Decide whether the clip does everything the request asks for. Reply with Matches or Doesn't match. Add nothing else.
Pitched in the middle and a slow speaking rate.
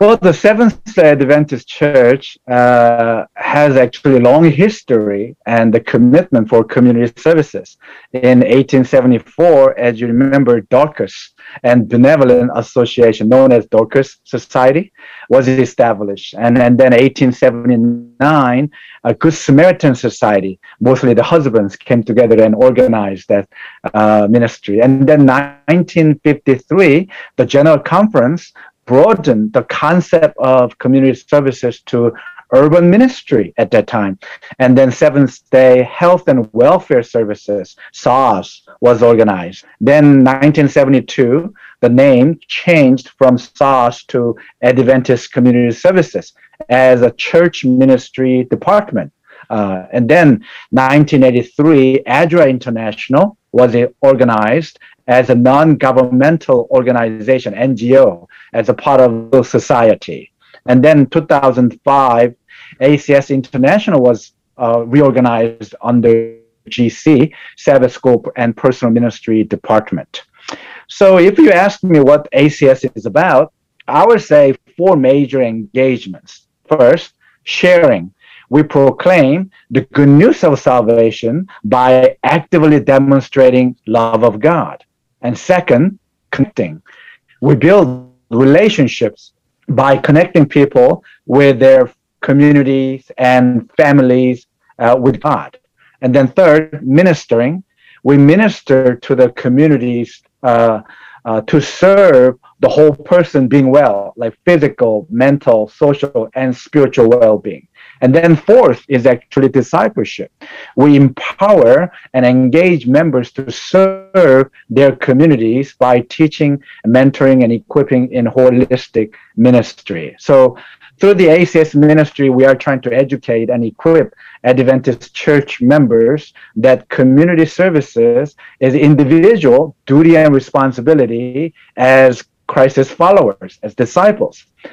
Doesn't match